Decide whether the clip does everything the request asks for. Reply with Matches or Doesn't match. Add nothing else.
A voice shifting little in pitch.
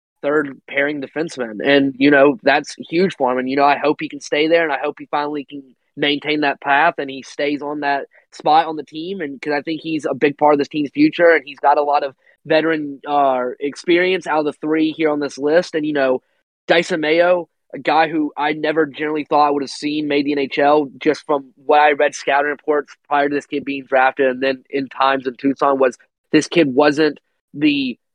Matches